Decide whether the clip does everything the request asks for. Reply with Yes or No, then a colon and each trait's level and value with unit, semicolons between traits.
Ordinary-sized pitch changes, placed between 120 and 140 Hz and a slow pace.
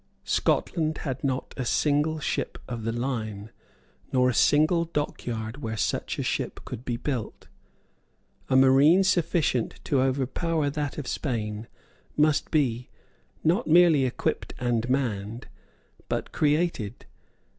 Yes: average, 4.5 semitones; low, 135 Hz; slow, 125 wpm